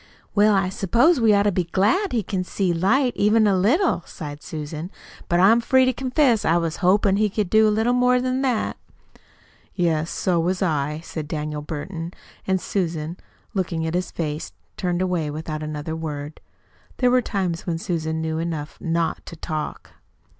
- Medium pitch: Yes, medium, 180 Hz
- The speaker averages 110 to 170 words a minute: No, average, 180 wpm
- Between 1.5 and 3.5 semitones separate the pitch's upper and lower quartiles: No, average, 5.0 semitones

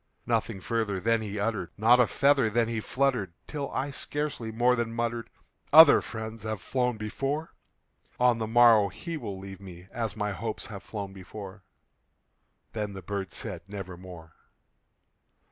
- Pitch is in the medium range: No, low, 110 Hz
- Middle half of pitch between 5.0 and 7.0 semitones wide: No, average, 3.4 semitones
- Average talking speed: Yes, average, 155 wpm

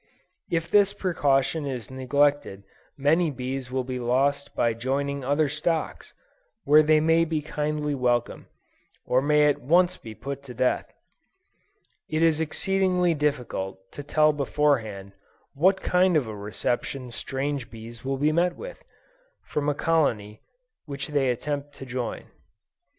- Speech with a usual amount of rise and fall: Yes, average, 3.4 semitones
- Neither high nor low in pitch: Yes, medium, 145 Hz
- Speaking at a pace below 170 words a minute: Yes, average, 140 wpm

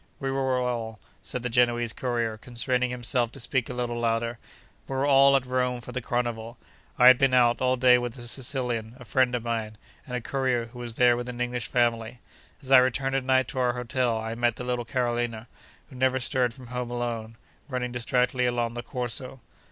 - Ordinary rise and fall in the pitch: No, narrow, 1.3 semitones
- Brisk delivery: Yes, fast, 210 wpm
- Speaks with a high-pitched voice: No, low, 125 Hz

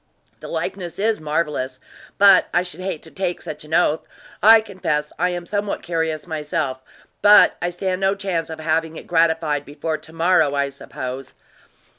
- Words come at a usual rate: Yes, average, 170 wpm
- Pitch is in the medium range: Yes, medium, 165 Hz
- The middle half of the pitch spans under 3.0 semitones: No, average, 3.4 semitones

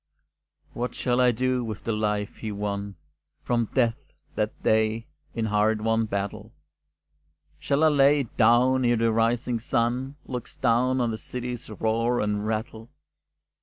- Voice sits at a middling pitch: No, low, 115 Hz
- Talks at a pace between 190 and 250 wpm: No, average, 155 wpm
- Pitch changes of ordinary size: No, narrow, 2.3 semitones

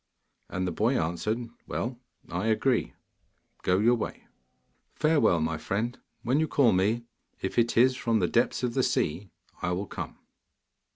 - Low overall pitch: Yes, low, 115 Hz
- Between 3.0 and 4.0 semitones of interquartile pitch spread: No, average, 4.8 semitones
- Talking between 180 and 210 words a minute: No, average, 160 wpm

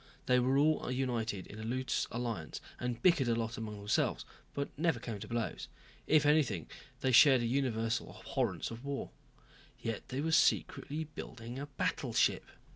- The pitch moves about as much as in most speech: Yes, average, 3.6 semitones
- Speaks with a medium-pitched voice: No, low, 125 Hz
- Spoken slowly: No, average, 165 wpm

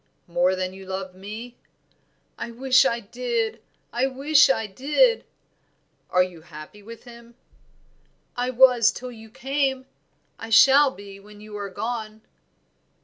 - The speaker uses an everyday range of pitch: Yes, average, 4.4 semitones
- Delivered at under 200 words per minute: Yes, average, 140 wpm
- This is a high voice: Yes, high, 230 Hz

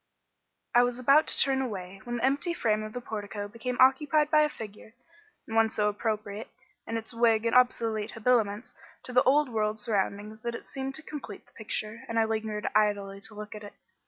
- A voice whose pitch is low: No, high, 225 Hz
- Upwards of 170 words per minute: Yes, fast, 205 wpm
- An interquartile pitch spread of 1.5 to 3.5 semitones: Yes, average, 2.9 semitones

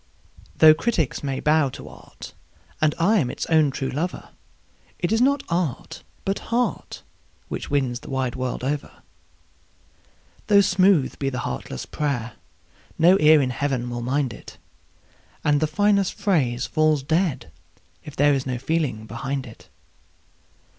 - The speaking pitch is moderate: Yes, medium, 145 Hz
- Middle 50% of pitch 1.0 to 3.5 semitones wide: No, average, 4.5 semitones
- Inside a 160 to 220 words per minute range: No, average, 145 wpm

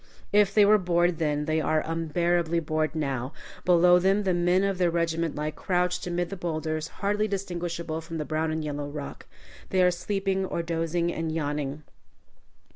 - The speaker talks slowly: No, average, 175 wpm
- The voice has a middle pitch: Yes, medium, 170 Hz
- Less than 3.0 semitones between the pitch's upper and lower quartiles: Yes, narrow, 2.4 semitones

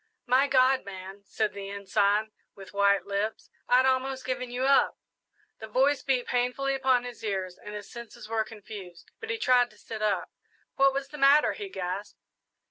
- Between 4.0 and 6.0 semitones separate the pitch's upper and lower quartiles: Yes, average, 4.6 semitones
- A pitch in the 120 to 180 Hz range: No, high, 235 Hz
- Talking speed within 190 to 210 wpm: No, average, 180 wpm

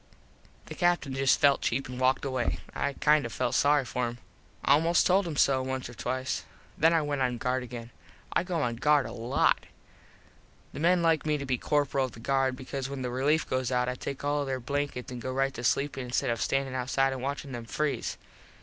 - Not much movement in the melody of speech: Yes, narrow, 2.3 semitones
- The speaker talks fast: Yes, fast, 220 wpm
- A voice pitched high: No, low, 135 Hz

